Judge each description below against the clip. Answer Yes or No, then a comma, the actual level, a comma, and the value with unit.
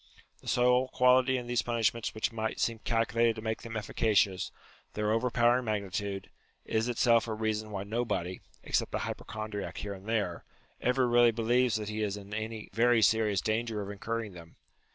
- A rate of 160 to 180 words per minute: Yes, average, 175 wpm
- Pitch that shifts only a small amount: Yes, narrow, 2.1 semitones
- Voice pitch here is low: Yes, low, 110 Hz